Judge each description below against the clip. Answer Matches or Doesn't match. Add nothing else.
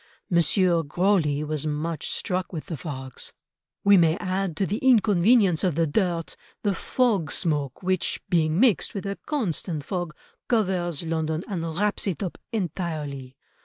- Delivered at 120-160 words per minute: Matches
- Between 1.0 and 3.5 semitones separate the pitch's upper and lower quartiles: Doesn't match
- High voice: Doesn't match